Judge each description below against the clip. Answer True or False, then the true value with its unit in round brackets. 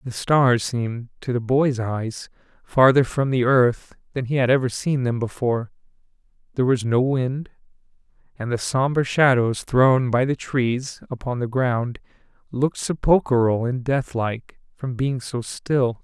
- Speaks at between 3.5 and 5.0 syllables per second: True (4.2 syllables/s)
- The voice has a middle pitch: False (125 Hz)